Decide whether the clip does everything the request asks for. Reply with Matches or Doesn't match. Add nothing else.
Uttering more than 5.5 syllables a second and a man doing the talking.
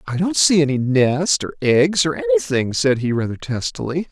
Doesn't match